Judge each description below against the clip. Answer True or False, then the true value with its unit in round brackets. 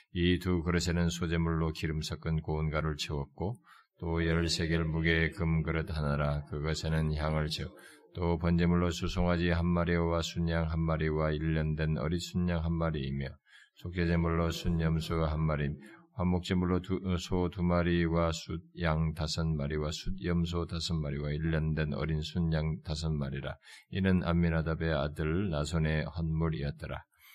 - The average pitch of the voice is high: False (80 Hz)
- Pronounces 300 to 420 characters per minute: True (315 characters per minute)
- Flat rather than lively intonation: True (1.7 semitones)